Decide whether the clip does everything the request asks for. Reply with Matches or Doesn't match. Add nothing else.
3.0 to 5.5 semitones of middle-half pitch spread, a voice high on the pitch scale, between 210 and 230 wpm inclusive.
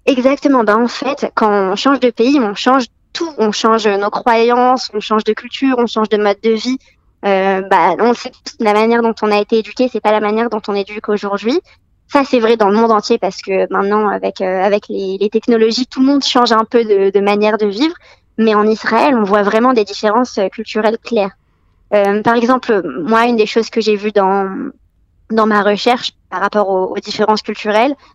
Doesn't match